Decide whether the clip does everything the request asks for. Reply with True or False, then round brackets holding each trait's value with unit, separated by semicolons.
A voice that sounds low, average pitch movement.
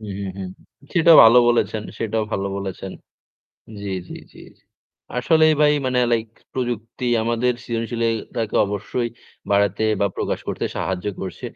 True (115 Hz; 3.5 semitones)